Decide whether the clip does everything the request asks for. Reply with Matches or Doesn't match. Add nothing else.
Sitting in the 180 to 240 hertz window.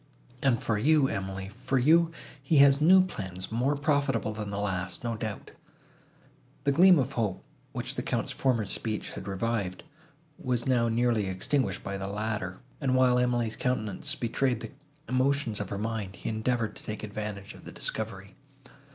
Doesn't match